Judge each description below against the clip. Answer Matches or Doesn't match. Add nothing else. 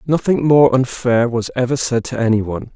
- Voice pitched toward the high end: Doesn't match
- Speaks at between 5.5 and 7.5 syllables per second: Doesn't match